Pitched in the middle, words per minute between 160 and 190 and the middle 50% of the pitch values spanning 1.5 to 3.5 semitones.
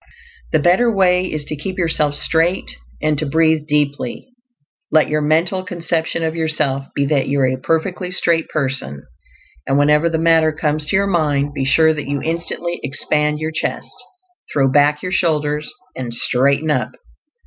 Yes: medium, 155 Hz; average, 170 wpm; narrow, 2.4 semitones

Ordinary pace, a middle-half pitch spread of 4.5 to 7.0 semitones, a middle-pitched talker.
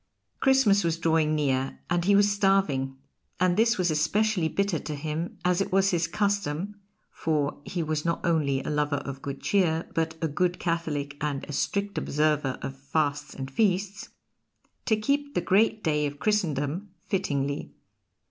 Yes: average, 165 wpm; average, 5.2 semitones; medium, 165 Hz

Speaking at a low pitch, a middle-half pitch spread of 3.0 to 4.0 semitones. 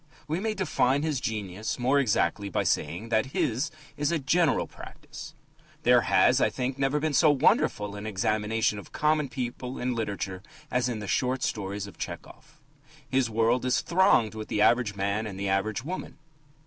No: low, 120 Hz; average, 4.8 semitones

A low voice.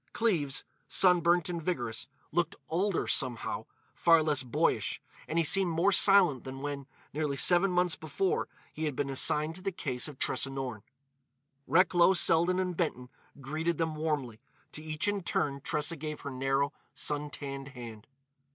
No: medium, 155 Hz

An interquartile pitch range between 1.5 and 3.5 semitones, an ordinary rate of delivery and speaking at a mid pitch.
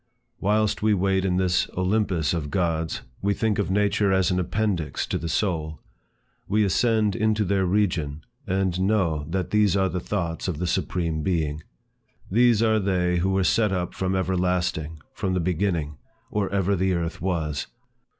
No: average, 3.1 semitones; average, 170 wpm; very low, 95 Hz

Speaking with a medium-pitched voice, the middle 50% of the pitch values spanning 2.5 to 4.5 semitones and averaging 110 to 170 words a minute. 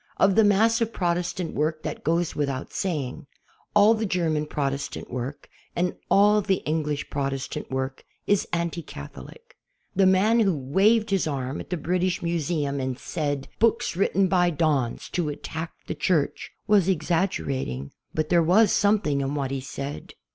No: medium, 165 Hz; average, 5.2 semitones; average, 160 wpm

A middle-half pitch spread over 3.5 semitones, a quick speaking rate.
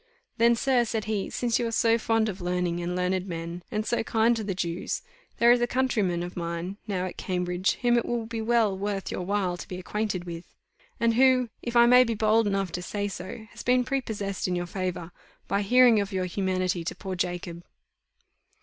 Yes: average, 4.3 semitones; fast, 215 wpm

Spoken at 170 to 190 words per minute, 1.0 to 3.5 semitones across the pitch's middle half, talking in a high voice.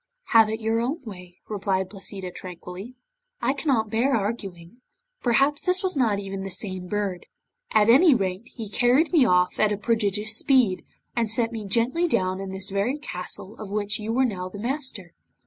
No: average, 180 wpm; average, 4.1 semitones; high, 215 Hz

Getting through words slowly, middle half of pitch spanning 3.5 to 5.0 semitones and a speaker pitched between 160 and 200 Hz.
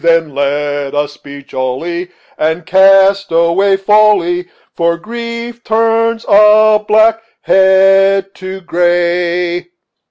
Yes: slow, 100 wpm; average, 3.8 semitones; high, 190 Hz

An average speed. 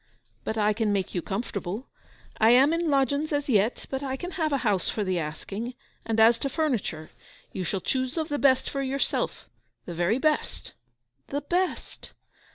Yes: average, 175 wpm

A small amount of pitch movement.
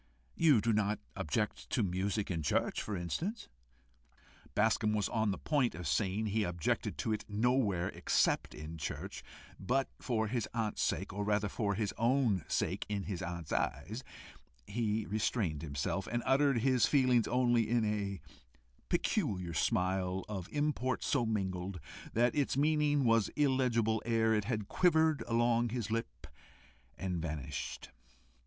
No: average, 4.2 semitones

